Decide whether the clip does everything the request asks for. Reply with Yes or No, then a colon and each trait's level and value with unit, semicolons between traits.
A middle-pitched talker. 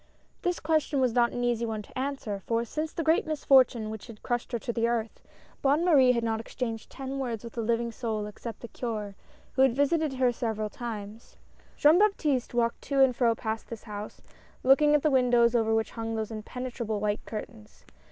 No: high, 235 Hz